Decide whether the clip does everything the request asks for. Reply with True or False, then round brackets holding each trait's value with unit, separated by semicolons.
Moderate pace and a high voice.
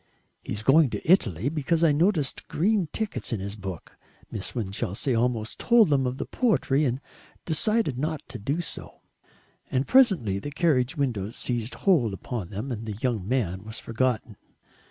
False (165 wpm; 130 Hz)